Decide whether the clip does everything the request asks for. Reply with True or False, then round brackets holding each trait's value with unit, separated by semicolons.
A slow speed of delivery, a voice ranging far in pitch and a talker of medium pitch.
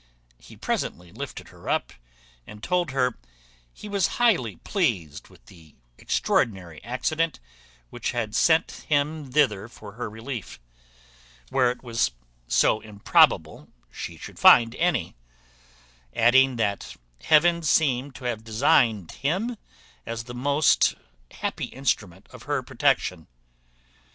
False (120 wpm; 5.8 semitones; 125 Hz)